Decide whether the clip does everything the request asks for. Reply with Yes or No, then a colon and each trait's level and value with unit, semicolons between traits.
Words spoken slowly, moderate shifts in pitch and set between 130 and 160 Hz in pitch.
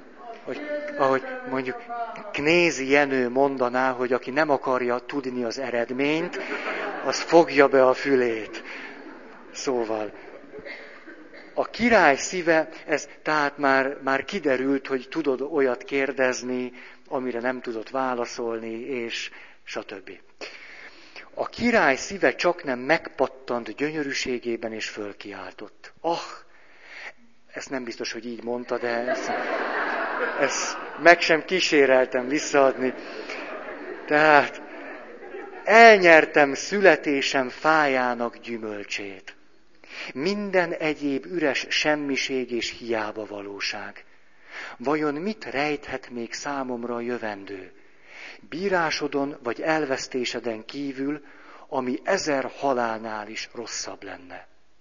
Yes: slow, 100 wpm; average, 4.0 semitones; low, 135 Hz